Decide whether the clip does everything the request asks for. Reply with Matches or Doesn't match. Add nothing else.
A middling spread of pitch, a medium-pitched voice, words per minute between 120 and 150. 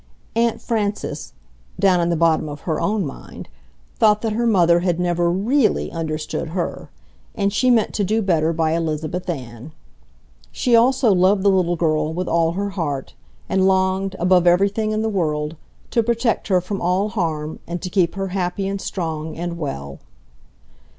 Doesn't match